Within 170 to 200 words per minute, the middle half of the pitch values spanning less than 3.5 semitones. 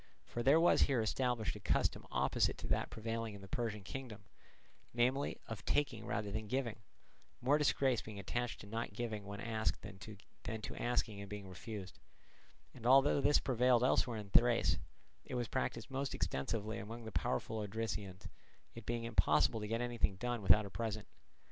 Yes: average, 175 wpm; average, 2.9 semitones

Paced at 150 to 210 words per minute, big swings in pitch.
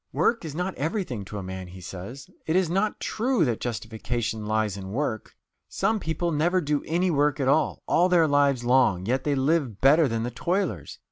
Yes: average, 200 wpm; wide, 7.2 semitones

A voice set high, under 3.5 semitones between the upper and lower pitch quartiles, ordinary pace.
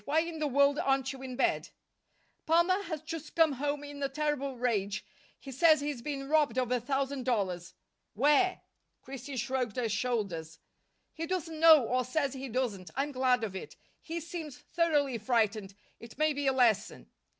No: very high, 270 Hz; average, 3.8 semitones; average, 175 wpm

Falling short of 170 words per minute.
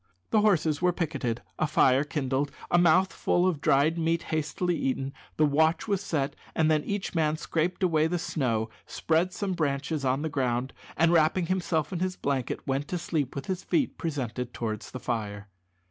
No: average, 180 wpm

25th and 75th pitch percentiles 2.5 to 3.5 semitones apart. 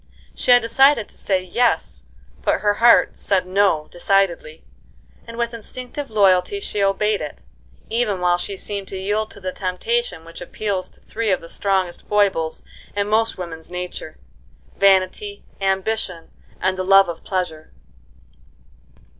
Yes: average, 3.1 semitones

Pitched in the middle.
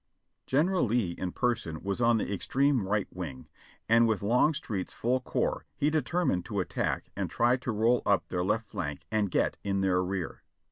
No: low, 105 Hz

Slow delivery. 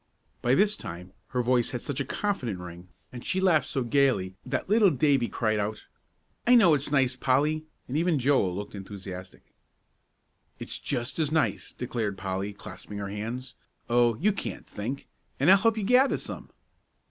No: average, 170 wpm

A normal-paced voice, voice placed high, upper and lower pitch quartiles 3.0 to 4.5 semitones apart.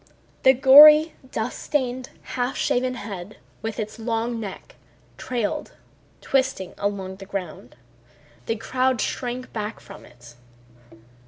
No: slow, 115 wpm; high, 230 Hz; average, 4.1 semitones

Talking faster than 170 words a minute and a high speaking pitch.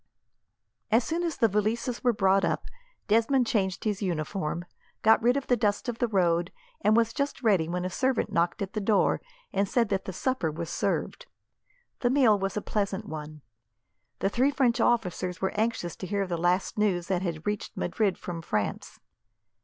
Yes: average, 185 wpm; high, 205 Hz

